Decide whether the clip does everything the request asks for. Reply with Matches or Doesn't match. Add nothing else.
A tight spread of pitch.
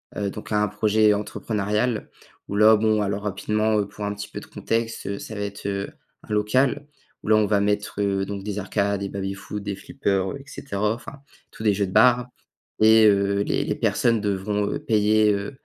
Matches